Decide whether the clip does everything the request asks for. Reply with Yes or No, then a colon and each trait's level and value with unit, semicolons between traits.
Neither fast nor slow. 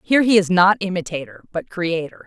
Yes: average, 185 wpm